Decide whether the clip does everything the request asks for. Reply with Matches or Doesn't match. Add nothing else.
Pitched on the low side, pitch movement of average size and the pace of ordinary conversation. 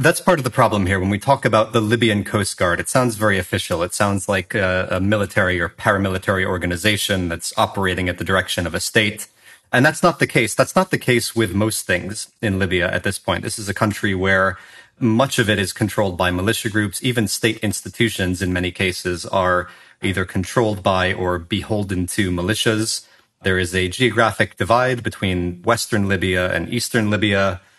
Matches